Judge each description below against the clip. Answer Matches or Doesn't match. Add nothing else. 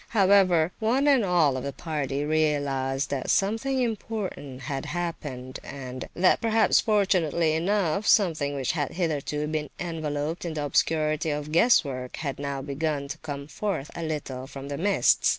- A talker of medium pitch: Matches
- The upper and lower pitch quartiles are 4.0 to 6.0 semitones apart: Matches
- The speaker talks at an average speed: Matches